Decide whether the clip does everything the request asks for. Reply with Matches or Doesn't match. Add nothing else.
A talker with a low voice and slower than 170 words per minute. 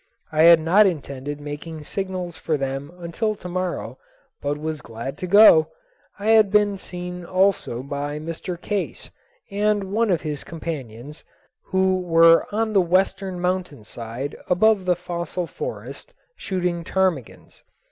Doesn't match